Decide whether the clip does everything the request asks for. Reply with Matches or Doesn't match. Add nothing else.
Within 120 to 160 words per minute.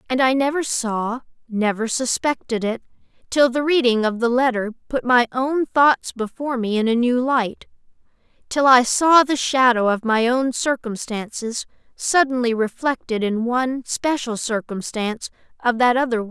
Matches